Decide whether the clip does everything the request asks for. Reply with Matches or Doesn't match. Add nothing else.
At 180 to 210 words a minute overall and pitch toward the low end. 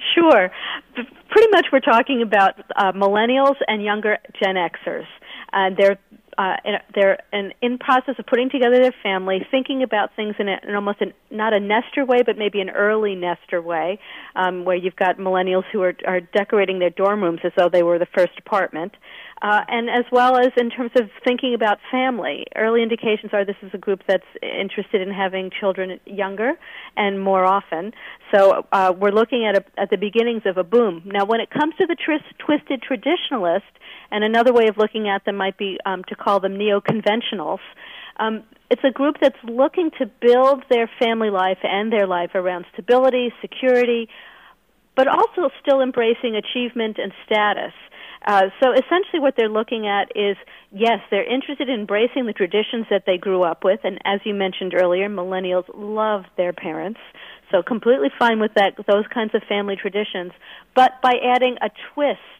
Doesn't match